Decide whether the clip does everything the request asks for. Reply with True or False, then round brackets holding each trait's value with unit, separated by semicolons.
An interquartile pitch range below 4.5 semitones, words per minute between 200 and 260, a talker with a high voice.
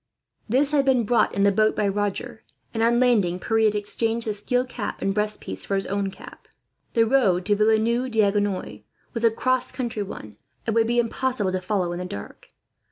True (3.0 semitones; 205 wpm; 215 Hz)